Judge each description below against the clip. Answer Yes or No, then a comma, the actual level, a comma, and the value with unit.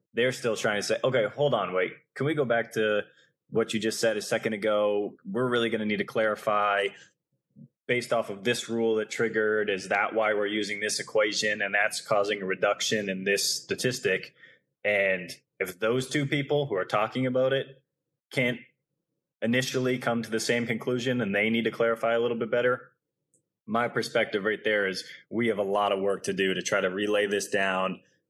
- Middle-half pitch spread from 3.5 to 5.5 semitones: No, average, 3.0 semitones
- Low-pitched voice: Yes, low, 110 Hz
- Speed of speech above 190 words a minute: Yes, average, 200 wpm